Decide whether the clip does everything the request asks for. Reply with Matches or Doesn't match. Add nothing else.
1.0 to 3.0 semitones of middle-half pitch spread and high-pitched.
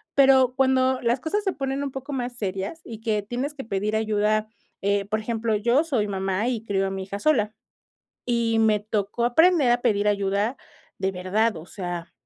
Doesn't match